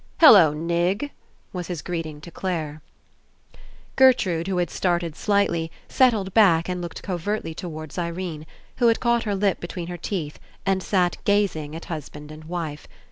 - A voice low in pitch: No, medium, 175 Hz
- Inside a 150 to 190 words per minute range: Yes, average, 160 wpm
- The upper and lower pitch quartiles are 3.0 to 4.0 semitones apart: Yes, average, 3.4 semitones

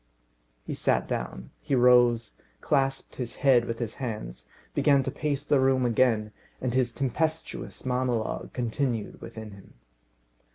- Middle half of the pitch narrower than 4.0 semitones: Yes, average, 2.8 semitones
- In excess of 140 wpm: No, slow, 135 wpm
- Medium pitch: No, low, 125 Hz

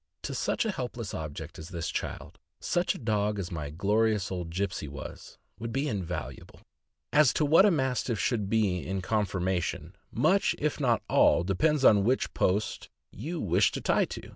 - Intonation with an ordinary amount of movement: No, wide, 6.2 semitones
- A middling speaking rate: Yes, average, 175 wpm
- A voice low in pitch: Yes, low, 105 Hz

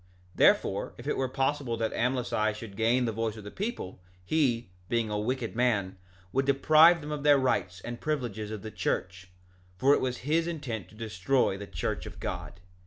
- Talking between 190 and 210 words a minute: Yes, average, 195 wpm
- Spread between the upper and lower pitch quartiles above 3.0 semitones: Yes, average, 4.2 semitones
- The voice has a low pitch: Yes, low, 120 Hz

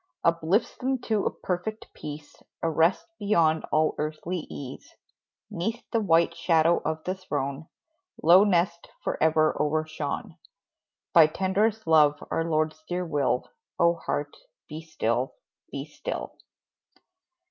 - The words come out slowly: Yes, slow, 125 wpm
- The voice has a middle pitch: Yes, medium, 165 Hz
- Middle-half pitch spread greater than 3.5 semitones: No, average, 2.9 semitones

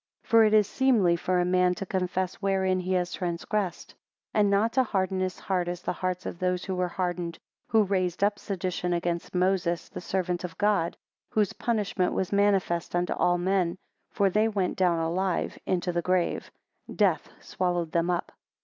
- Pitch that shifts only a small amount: Yes, narrow, 2.0 semitones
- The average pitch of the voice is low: No, medium, 185 Hz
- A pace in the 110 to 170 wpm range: No, average, 185 wpm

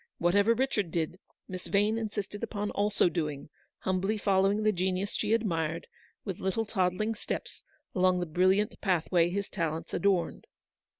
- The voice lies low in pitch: No, high, 190 Hz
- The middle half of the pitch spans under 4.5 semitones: Yes, average, 2.9 semitones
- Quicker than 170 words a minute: No, average, 145 wpm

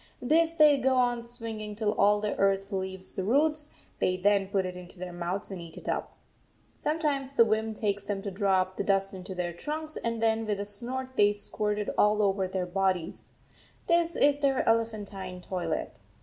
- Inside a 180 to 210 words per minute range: Yes, average, 195 wpm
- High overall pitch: Yes, high, 210 Hz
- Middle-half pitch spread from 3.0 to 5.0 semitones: Yes, average, 4.3 semitones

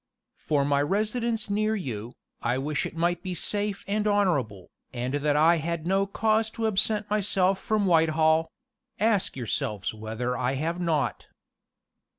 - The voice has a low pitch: No, medium, 170 Hz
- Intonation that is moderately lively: No, wide, 6.5 semitones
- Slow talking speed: No, average, 150 wpm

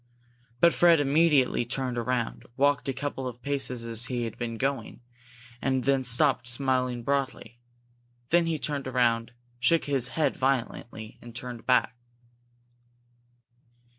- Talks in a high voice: No, low, 130 Hz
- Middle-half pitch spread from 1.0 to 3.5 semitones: Yes, average, 2.7 semitones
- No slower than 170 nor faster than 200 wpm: No, slow, 135 wpm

